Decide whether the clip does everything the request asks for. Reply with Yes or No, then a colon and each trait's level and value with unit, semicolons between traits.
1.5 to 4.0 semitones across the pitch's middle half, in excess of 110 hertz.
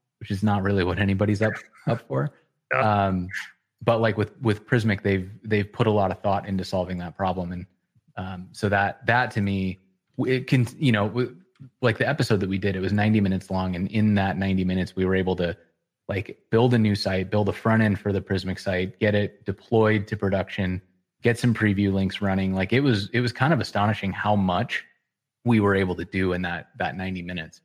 No: average, 3.0 semitones; low, 100 Hz